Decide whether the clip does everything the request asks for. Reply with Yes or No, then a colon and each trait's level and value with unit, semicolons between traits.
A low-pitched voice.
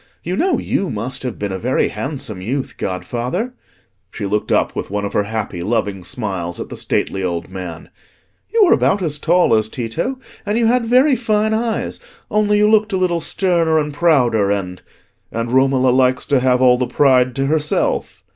Yes: low, 130 Hz